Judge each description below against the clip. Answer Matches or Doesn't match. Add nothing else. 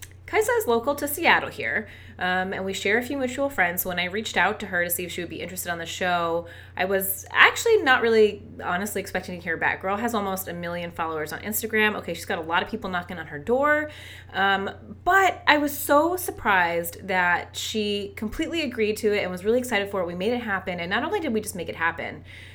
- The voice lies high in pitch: Matches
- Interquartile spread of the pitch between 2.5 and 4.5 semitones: Doesn't match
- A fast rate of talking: Matches